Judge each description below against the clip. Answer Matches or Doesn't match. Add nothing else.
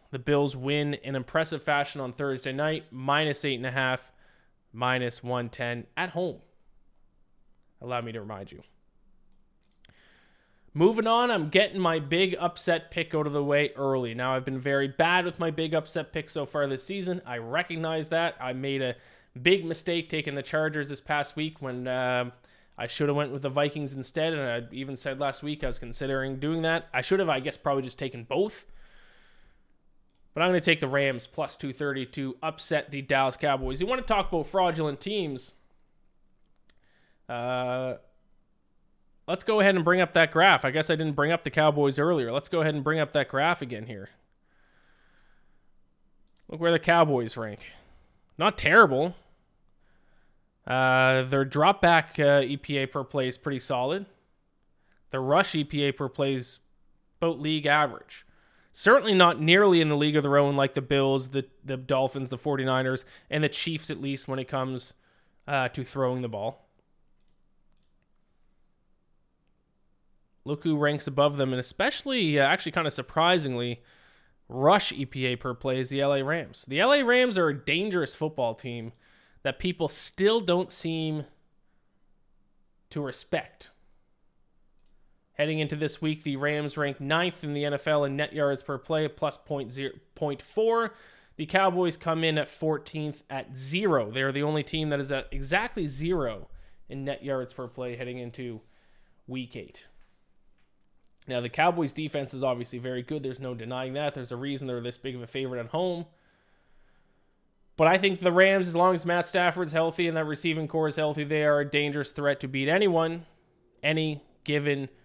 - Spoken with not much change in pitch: Doesn't match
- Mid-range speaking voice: Matches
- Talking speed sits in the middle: Matches